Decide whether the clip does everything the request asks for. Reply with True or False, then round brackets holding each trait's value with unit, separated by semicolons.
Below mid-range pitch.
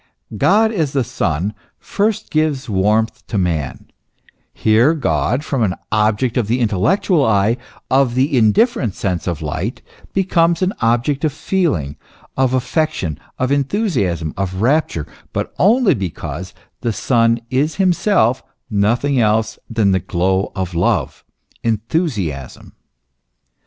True (115 Hz)